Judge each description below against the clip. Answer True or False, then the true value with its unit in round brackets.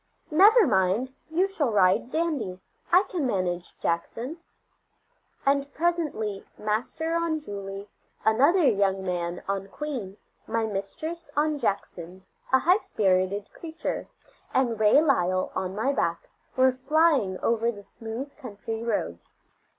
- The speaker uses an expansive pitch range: True (7.6 semitones)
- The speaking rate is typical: False (125 wpm)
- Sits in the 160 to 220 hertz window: False (230 Hz)